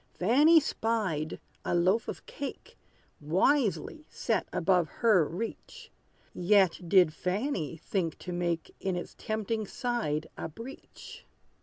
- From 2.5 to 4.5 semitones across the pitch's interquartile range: No, average, 5.1 semitones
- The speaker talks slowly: Yes, slow, 120 wpm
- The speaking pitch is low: No, high, 190 Hz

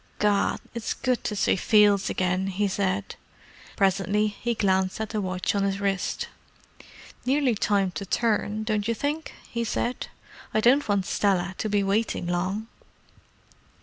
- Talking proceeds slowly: No, average, 150 wpm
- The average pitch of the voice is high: Yes, high, 205 Hz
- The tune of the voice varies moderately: No, narrow, 2.2 semitones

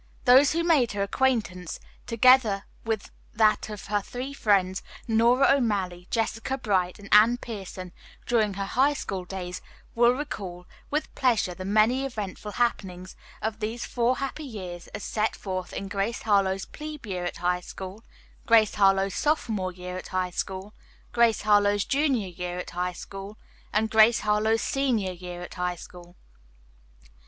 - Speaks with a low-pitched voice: No, high, 210 Hz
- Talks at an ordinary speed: Yes, average, 155 wpm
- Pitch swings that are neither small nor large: Yes, average, 4.2 semitones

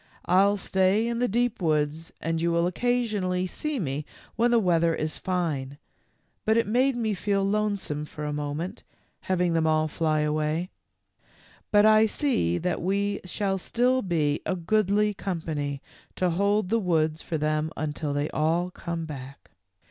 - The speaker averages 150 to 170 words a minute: Yes, average, 160 wpm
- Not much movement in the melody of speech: No, average, 5.1 semitones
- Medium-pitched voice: Yes, medium, 180 Hz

